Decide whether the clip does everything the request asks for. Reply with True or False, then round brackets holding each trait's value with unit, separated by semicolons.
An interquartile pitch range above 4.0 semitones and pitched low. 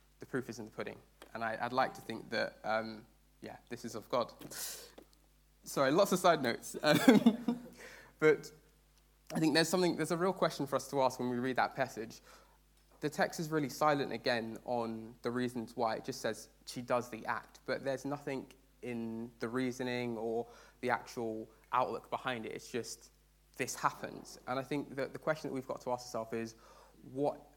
True (4.5 semitones; 130 Hz)